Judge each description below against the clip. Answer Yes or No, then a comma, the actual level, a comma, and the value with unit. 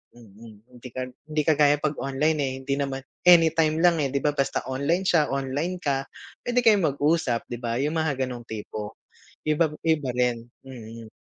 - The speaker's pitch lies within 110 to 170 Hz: Yes, medium, 140 Hz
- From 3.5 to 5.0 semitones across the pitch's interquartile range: Yes, average, 3.9 semitones